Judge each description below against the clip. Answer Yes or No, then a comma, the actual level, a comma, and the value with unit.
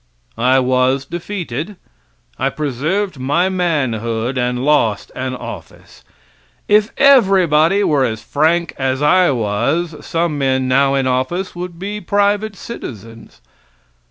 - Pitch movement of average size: No, wide, 6.0 semitones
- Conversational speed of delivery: No, slow, 120 wpm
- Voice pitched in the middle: Yes, medium, 150 Hz